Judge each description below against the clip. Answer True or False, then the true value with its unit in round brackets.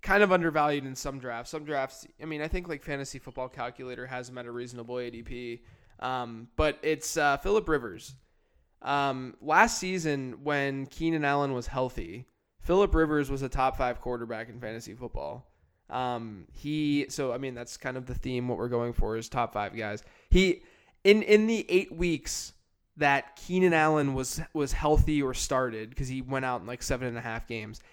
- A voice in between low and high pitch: False (130 Hz)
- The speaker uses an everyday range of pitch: True (3.8 semitones)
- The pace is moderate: True (190 wpm)